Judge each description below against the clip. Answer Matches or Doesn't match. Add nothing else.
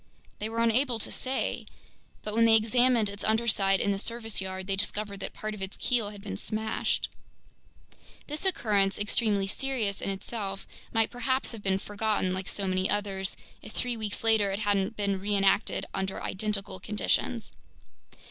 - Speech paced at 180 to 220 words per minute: Doesn't match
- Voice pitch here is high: Matches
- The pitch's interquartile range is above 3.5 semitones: Doesn't match